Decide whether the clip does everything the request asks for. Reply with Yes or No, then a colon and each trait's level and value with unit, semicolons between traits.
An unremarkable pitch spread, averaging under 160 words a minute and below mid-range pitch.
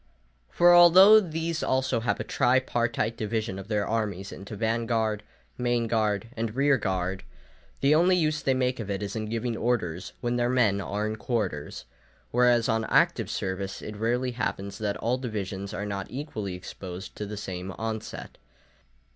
No: average, 3.7 semitones; average, 170 wpm; low, 110 Hz